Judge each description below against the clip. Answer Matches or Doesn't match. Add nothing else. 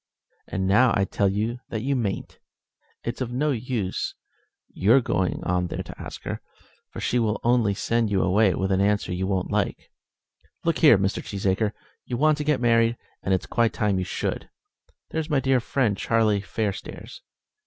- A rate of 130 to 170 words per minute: Doesn't match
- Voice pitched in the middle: Doesn't match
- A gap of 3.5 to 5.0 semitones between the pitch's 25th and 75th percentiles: Matches